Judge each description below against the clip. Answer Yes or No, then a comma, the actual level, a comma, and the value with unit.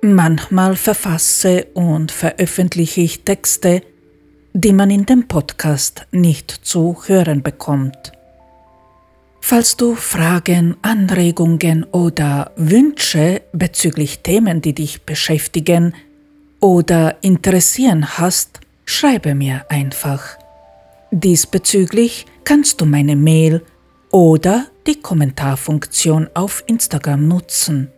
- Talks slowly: Yes, slow, 90 wpm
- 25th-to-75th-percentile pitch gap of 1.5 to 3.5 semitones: No, average, 4.1 semitones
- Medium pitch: Yes, medium, 170 Hz